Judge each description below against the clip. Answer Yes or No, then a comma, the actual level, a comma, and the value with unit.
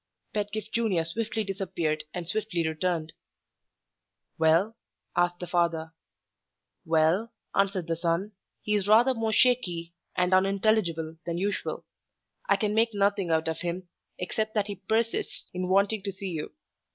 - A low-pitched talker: No, medium, 185 Hz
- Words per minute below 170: Yes, average, 140 wpm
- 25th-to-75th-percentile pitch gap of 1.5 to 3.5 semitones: No, average, 4.1 semitones